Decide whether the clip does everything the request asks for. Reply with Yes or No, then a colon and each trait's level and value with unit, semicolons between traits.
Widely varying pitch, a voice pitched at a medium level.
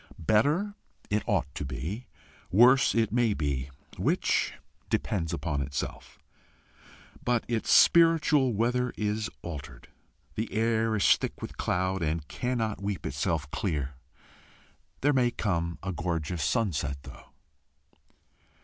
No: wide, 7.2 semitones; low, 100 Hz